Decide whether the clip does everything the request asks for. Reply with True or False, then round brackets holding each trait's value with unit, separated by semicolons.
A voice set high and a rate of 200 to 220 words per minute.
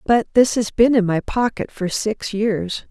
True (215 Hz; 205 wpm)